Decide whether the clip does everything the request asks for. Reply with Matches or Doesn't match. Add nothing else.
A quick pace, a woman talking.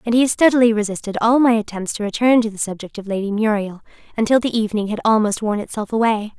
Matches